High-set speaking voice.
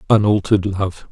No: low, 100 Hz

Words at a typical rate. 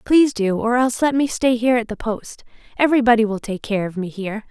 No: fast, 240 wpm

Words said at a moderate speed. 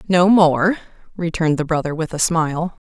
Yes: average, 170 wpm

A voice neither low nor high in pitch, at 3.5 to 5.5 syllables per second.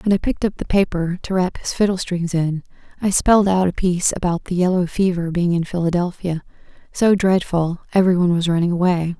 No: medium, 180 Hz; 6.0 syllables/s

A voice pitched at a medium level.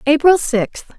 No: very high, 280 Hz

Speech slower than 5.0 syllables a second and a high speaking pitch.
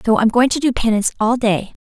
No: 6.4 syllables/s; high, 230 Hz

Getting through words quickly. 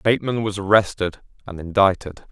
No: slow, 130 wpm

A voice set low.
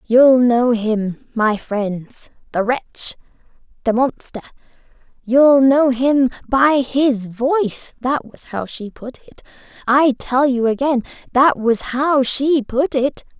No: very high, 250 Hz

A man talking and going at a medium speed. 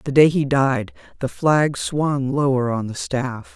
No: female; average, 185 wpm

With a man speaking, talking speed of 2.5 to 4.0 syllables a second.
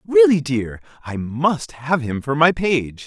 Yes: male; 3.7 syllables/s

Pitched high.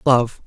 No: low, 120 Hz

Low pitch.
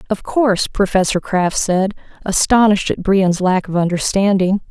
No: high, 195 Hz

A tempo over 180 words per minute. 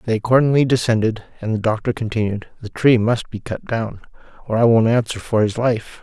Yes: average, 200 wpm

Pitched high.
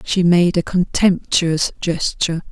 No: medium, 175 Hz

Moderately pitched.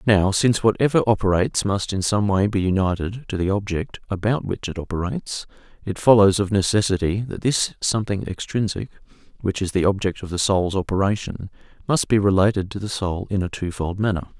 No: low, 100 Hz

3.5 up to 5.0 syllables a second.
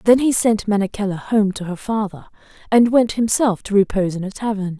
No: 5.5 syllables/s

